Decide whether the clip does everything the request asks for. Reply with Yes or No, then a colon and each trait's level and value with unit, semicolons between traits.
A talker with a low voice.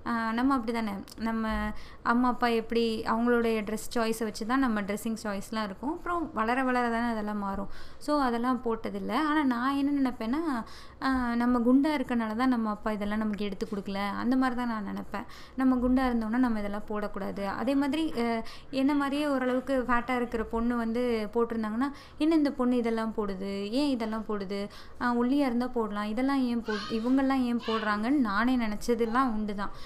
No: high, 235 Hz